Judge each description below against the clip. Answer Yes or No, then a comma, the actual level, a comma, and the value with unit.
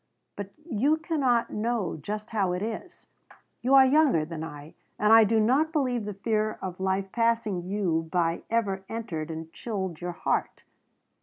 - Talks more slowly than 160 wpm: No, average, 165 wpm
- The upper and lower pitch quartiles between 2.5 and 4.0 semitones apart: No, average, 4.8 semitones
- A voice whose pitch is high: Yes, high, 210 Hz